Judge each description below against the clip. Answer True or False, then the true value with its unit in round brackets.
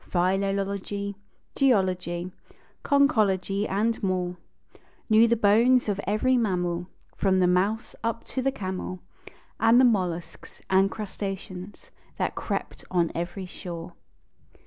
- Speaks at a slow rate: True (115 wpm)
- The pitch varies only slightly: False (3.3 semitones)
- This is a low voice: False (195 Hz)